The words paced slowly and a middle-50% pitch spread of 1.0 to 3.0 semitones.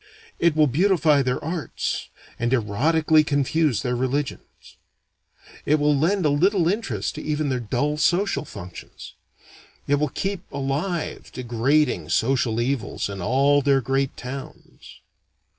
No: slow, 130 wpm; average, 3.7 semitones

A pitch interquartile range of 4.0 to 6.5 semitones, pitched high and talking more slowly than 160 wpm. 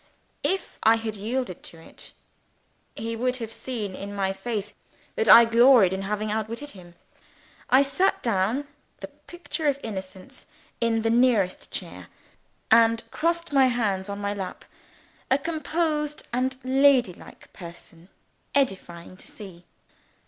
Yes: average, 5.1 semitones; high, 225 Hz; slow, 135 wpm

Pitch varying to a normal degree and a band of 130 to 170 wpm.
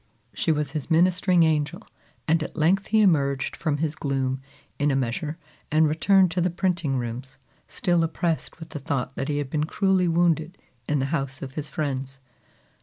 No: average, 3.7 semitones; average, 185 wpm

